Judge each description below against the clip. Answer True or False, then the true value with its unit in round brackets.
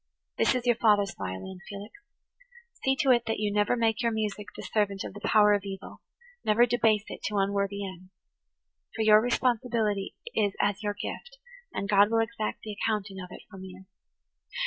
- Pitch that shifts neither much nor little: False (2.3 semitones)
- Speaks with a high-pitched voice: True (210 Hz)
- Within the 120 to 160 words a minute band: False (180 wpm)